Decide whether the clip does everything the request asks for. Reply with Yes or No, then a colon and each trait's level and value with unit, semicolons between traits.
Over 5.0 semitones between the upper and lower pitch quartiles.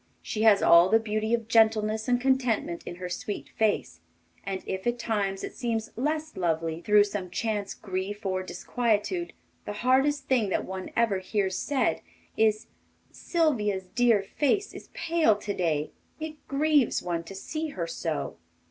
No: average, 4.7 semitones